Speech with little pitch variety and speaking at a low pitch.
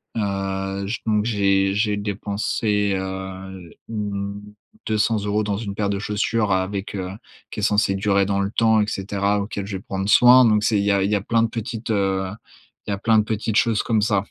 Yes: narrow, 1.6 semitones; low, 100 Hz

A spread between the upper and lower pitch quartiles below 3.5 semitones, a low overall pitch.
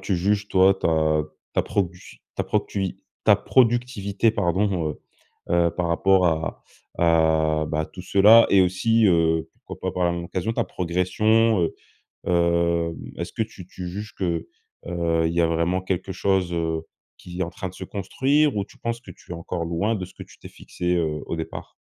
Yes: average, 2.9 semitones; very low, 90 Hz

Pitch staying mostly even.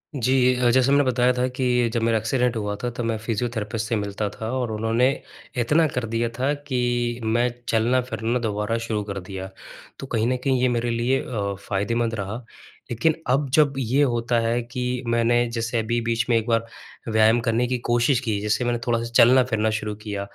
Yes: narrow, 2.1 semitones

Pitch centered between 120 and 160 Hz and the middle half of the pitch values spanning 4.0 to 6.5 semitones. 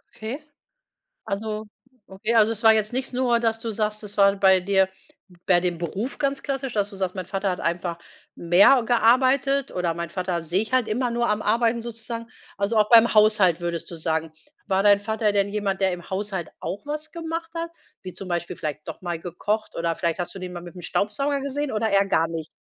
No: high, 205 Hz; average, 4.4 semitones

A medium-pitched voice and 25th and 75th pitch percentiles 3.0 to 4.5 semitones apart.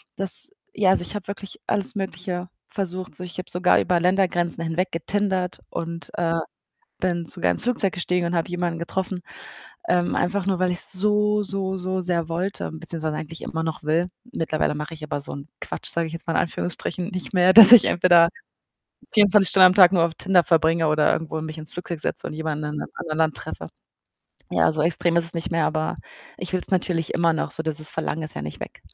No: medium, 175 Hz; narrow, 2.4 semitones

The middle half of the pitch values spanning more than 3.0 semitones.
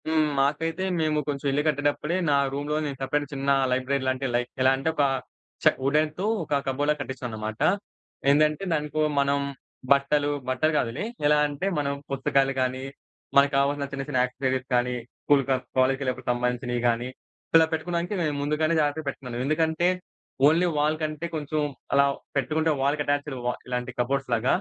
No: average, 2.7 semitones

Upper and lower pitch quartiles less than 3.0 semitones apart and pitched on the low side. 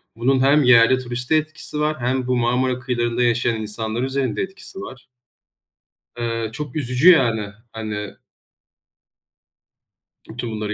Yes: narrow, 2.6 semitones; low, 125 Hz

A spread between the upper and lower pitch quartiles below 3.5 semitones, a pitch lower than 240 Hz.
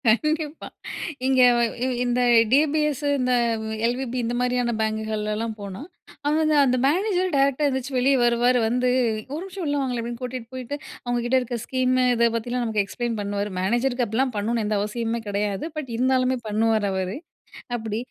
No: average, 3.0 semitones; high, 245 Hz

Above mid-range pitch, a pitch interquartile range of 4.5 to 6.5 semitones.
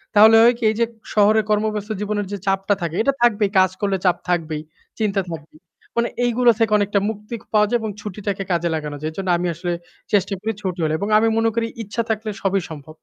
No: high, 205 Hz; average, 3.4 semitones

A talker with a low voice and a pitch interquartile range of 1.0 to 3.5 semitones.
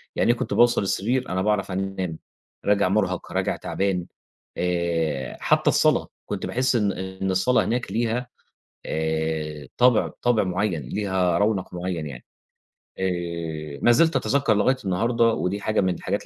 No: very low, 95 Hz; average, 4.9 semitones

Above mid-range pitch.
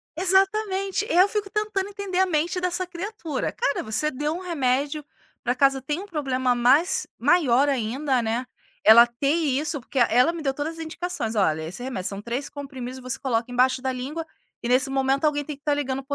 Yes: very high, 280 Hz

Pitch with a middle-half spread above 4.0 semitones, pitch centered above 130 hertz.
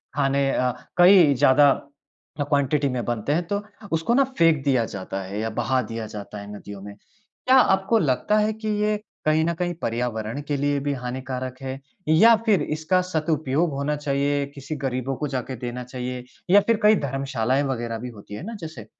Yes: average, 4.4 semitones; medium, 140 Hz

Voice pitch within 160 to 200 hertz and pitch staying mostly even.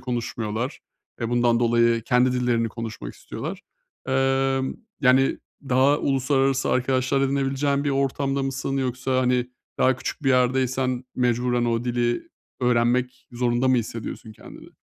No: low, 125 Hz; narrow, 1.8 semitones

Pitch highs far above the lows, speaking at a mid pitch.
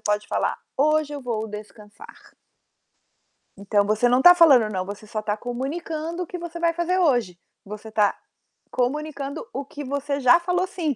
No: wide, 7.1 semitones; very high, 270 Hz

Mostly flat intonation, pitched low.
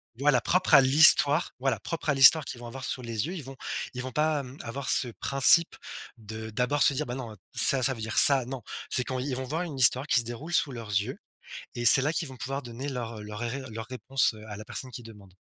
No: average, 3.2 semitones; low, 130 Hz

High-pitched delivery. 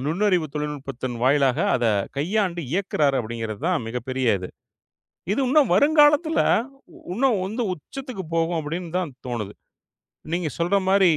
No: medium, 165 Hz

